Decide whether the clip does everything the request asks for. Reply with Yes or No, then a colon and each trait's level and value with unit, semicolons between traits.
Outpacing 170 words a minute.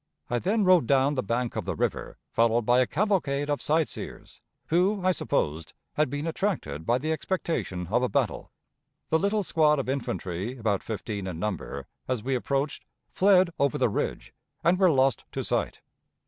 Yes: average, 180 wpm